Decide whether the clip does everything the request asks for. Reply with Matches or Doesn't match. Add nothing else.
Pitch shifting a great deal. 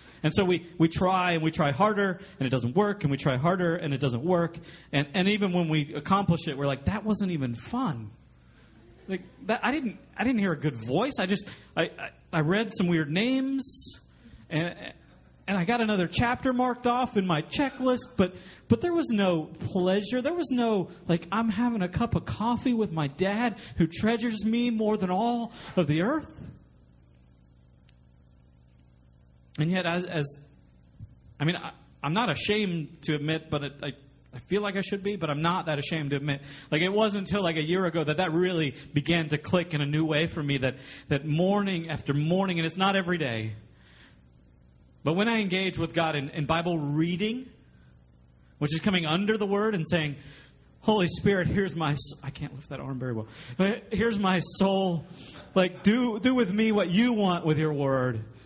Matches